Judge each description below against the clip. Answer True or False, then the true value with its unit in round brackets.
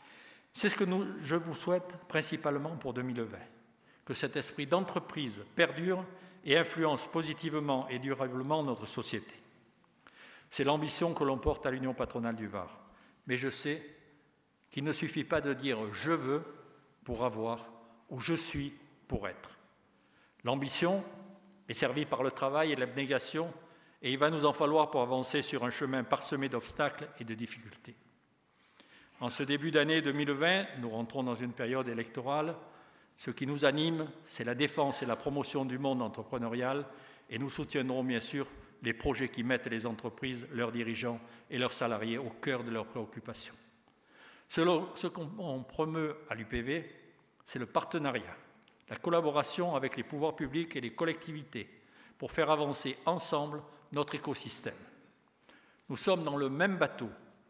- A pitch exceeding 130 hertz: True (140 Hz)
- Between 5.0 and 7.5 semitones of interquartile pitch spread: False (3.9 semitones)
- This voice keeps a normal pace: True (155 wpm)